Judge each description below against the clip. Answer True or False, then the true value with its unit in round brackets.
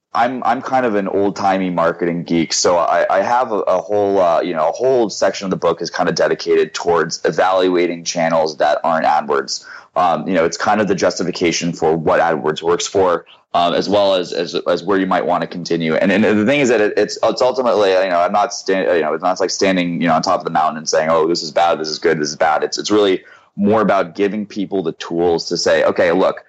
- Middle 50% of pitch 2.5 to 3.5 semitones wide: True (3.0 semitones)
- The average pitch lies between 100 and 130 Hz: False (90 Hz)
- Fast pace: True (255 wpm)